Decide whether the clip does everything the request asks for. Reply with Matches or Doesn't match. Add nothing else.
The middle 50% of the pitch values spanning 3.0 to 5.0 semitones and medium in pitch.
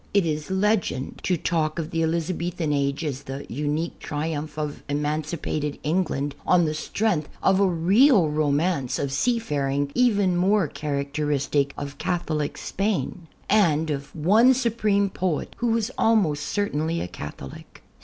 Matches